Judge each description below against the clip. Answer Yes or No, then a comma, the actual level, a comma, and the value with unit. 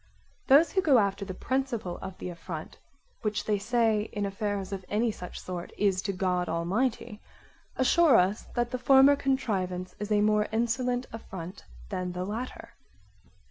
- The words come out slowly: No, average, 160 wpm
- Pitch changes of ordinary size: Yes, average, 4.6 semitones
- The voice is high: Yes, high, 210 Hz